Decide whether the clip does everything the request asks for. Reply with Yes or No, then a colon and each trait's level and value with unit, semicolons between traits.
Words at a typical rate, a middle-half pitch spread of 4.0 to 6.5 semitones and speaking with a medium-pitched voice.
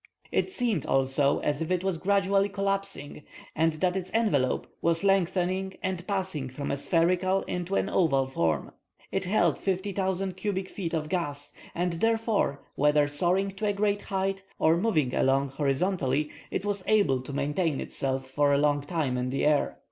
Yes: average, 170 wpm; average, 5.1 semitones; medium, 175 Hz